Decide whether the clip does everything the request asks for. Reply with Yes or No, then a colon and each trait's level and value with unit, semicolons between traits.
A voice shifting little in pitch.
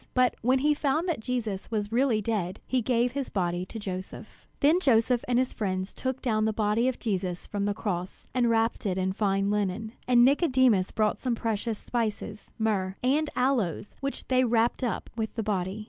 No: average, 3.8 semitones